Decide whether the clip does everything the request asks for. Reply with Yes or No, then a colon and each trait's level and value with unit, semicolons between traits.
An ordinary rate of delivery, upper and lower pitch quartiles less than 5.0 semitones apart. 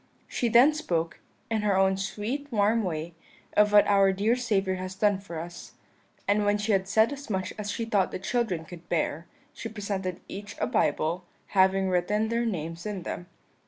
Yes: average, 190 wpm; average, 2.8 semitones